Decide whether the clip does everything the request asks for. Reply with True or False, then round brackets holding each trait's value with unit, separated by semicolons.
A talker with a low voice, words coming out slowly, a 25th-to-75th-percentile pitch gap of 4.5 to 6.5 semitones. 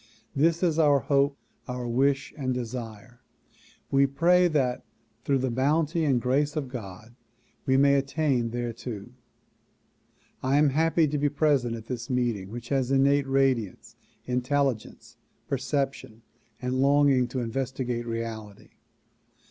False (130 Hz; 130 wpm; 2.8 semitones)